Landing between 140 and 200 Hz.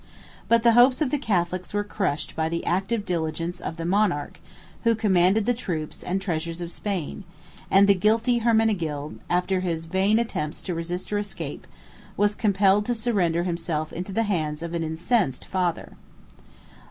Yes: medium, 185 Hz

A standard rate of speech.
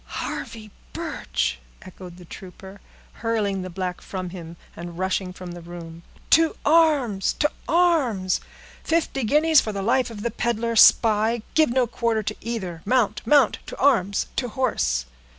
Yes: average, 150 wpm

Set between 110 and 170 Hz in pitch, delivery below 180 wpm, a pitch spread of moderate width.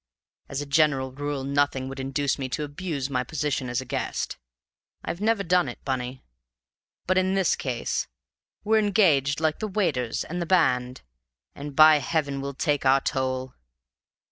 Yes: medium, 140 Hz; average, 165 wpm; average, 3.7 semitones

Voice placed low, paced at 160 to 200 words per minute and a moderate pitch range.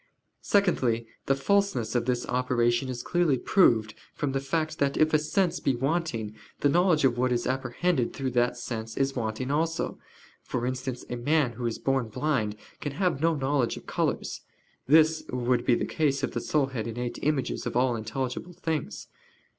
Yes: low, 130 Hz; average, 185 wpm; average, 4.3 semitones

